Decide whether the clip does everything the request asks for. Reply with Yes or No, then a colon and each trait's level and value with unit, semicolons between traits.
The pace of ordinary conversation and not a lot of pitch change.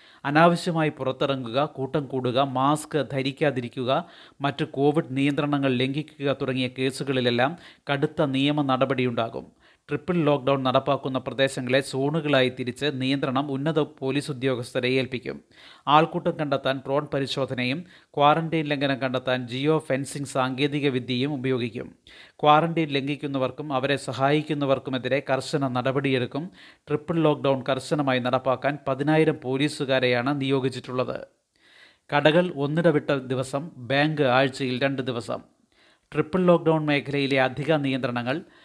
Yes: average, 100 wpm; narrow, 2.2 semitones